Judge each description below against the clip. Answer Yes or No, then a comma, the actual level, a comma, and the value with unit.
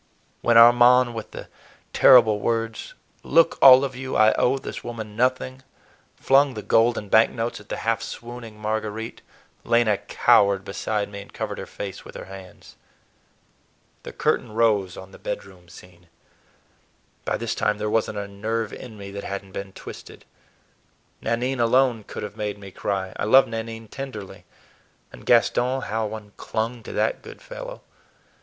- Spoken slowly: No, average, 165 wpm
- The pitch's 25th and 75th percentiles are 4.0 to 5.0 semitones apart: No, average, 2.9 semitones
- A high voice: No, low, 110 Hz